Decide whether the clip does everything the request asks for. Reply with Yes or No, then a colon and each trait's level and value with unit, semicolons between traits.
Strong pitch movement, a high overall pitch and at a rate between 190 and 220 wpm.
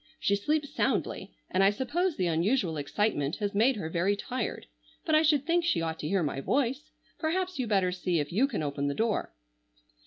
Yes: wide, 8.8 semitones; high, 205 Hz; fast, 205 wpm